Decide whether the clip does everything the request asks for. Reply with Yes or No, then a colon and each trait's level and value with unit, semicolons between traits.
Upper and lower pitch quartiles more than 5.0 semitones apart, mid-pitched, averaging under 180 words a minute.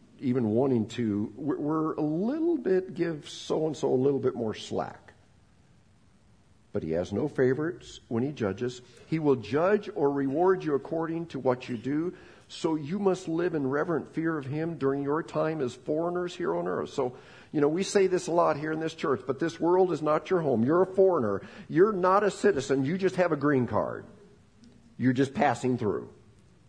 No: wide, 5.6 semitones; medium, 150 Hz; average, 200 wpm